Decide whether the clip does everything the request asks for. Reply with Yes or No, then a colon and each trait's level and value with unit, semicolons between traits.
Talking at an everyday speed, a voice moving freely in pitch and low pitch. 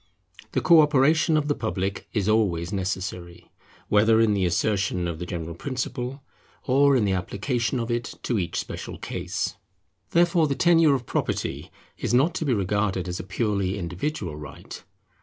Yes: average, 165 wpm; wide, 6.7 semitones; low, 105 Hz